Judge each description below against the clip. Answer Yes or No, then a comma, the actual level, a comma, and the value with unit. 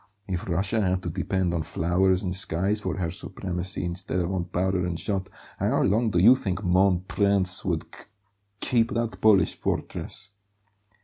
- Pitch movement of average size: No, narrow, 2.1 semitones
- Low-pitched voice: Yes, very low, 95 Hz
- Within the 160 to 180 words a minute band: Yes, average, 170 wpm